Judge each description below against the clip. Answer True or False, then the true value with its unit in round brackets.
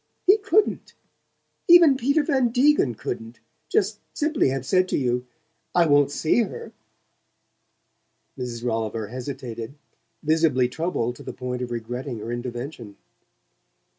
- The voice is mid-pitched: False (130 Hz)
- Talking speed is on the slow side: True (125 wpm)